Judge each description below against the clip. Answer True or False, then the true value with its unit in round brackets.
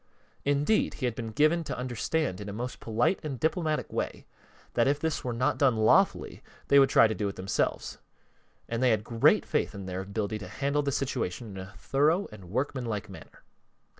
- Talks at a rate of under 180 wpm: False (195 wpm)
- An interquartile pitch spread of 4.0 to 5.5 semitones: True (5.1 semitones)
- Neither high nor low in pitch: False (120 Hz)